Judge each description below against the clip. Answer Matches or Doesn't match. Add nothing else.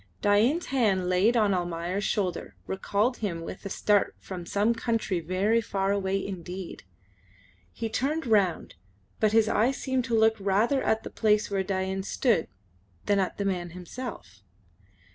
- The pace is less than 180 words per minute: Matches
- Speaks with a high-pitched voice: Matches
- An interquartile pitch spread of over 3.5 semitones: Doesn't match